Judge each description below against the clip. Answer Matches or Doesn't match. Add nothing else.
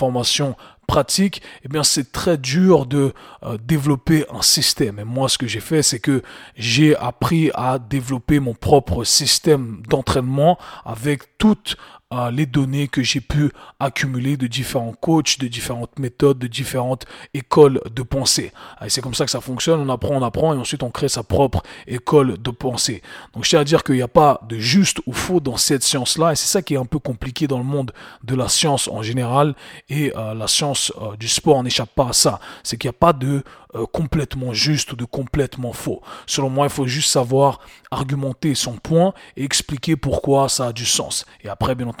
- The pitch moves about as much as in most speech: Matches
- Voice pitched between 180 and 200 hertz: Doesn't match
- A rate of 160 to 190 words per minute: Doesn't match